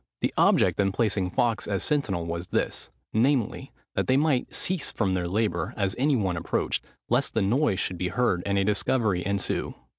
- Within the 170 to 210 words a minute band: Yes, average, 185 wpm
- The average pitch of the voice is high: No, low, 100 Hz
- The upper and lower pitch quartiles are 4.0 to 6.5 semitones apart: Yes, average, 5.0 semitones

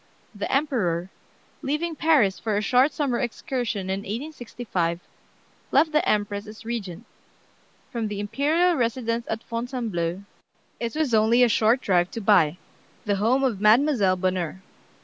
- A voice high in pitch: Yes, high, 225 Hz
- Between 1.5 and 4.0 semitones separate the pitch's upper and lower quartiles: No, average, 4.5 semitones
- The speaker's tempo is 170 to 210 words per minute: No, average, 140 wpm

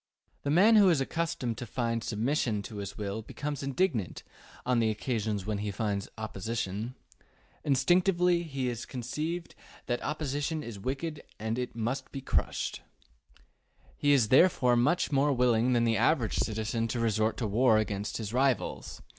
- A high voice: No, low, 120 Hz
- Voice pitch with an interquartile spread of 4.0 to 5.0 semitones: Yes, average, 4.6 semitones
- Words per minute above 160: No, average, 155 wpm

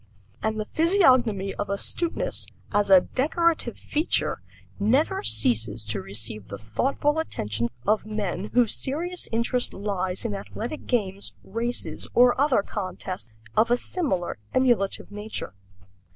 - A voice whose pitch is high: Yes, high, 215 Hz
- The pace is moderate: No, slow, 125 wpm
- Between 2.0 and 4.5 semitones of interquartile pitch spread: No, wide, 5.5 semitones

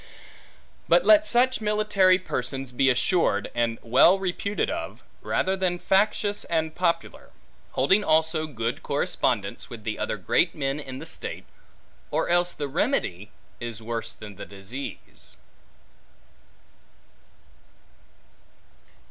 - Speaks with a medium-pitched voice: Yes, medium, 150 Hz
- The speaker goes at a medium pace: No, slow, 115 wpm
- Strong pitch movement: Yes, wide, 8.2 semitones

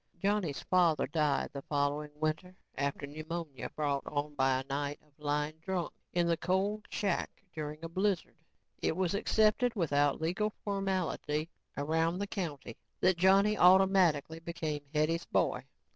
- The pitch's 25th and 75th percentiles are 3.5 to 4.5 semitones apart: Yes, average, 4.1 semitones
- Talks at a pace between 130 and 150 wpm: Yes, average, 145 wpm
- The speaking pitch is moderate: Yes, medium, 165 Hz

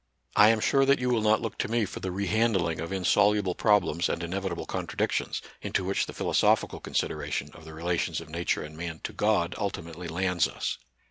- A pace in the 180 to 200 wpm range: Yes, average, 195 wpm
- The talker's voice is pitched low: Yes, very low, 95 Hz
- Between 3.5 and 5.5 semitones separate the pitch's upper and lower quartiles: Yes, average, 3.9 semitones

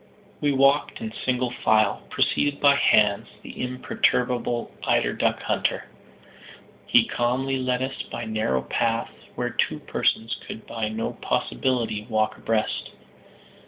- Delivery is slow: Yes, slow, 125 wpm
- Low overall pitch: Yes, low, 120 Hz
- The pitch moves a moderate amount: Yes, average, 3.1 semitones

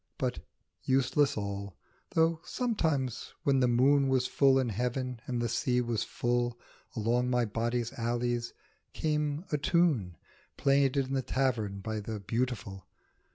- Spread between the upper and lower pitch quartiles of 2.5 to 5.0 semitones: Yes, average, 3.0 semitones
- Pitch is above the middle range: No, low, 125 Hz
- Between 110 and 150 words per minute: Yes, average, 140 wpm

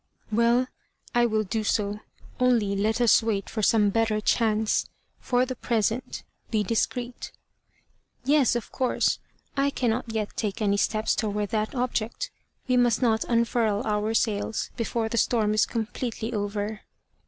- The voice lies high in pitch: Yes, high, 225 Hz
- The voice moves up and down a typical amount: No, narrow, 2.1 semitones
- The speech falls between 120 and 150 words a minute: Yes, average, 145 wpm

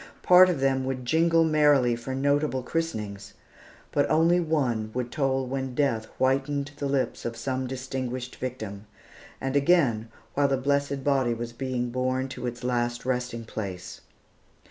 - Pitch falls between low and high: No, low, 130 Hz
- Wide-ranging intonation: No, average, 2.8 semitones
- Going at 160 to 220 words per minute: No, average, 150 wpm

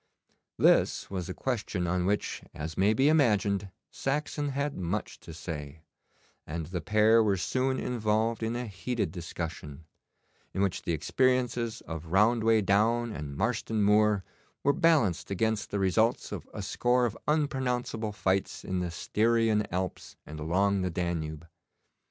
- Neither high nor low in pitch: No, low, 105 Hz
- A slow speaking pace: No, average, 145 wpm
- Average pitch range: Yes, average, 4.7 semitones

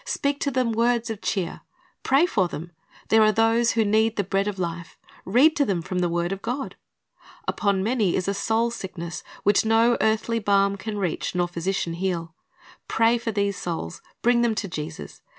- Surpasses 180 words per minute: Yes, average, 190 wpm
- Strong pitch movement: No, average, 4.1 semitones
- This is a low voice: No, high, 205 Hz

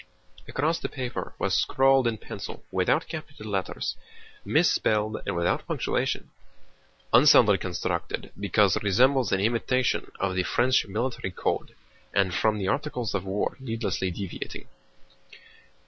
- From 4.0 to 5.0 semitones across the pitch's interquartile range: Yes, average, 4.7 semitones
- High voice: No, low, 110 Hz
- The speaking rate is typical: No, slow, 125 wpm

